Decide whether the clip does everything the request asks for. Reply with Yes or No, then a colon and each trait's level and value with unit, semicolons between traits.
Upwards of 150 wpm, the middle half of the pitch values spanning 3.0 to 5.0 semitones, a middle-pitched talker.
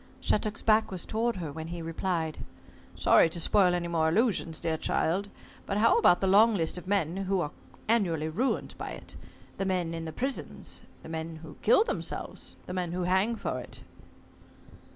Yes: average, 185 wpm; average, 4.0 semitones; medium, 180 Hz